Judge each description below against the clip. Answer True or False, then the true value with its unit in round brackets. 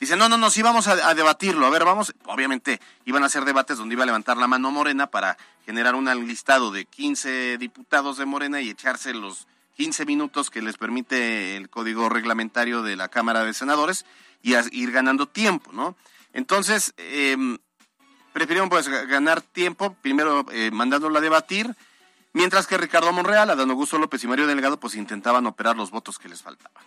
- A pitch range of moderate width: False (6.9 semitones)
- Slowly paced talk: False (185 wpm)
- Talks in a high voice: False (140 Hz)